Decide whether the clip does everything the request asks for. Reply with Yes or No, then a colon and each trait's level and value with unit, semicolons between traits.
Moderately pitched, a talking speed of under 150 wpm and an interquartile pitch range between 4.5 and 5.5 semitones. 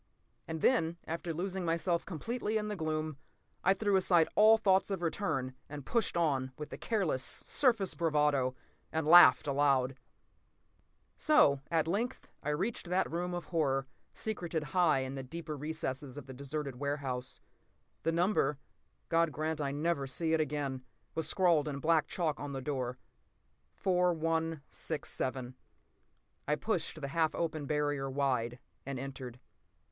No: medium, 155 Hz; average, 140 wpm; average, 4.0 semitones